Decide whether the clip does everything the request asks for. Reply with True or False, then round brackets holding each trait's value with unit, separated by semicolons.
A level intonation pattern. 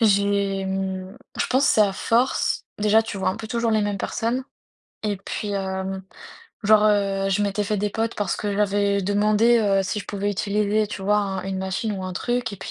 True (1.7 semitones)